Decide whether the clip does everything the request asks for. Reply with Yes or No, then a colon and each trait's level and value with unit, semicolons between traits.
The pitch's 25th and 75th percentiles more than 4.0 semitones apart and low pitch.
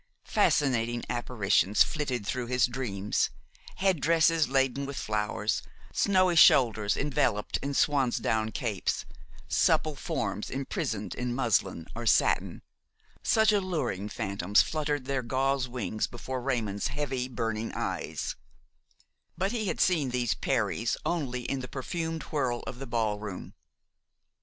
Yes: average, 4.6 semitones; low, 125 Hz